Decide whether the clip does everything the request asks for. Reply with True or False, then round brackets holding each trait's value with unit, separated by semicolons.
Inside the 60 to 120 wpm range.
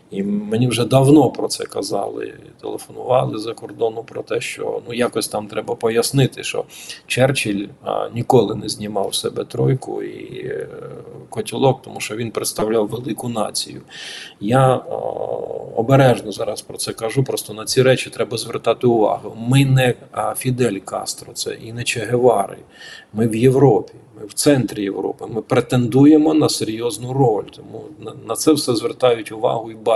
False (155 wpm)